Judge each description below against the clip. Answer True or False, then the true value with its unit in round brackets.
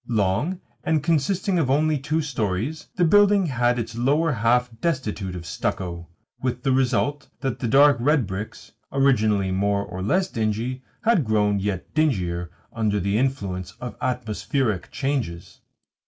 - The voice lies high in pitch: False (125 Hz)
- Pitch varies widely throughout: True (6.2 semitones)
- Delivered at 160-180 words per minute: False (145 wpm)